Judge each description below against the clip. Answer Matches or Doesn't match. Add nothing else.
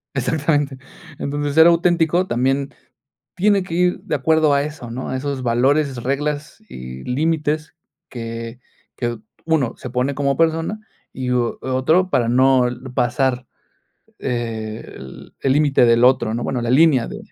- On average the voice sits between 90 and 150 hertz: Matches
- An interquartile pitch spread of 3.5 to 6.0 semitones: Matches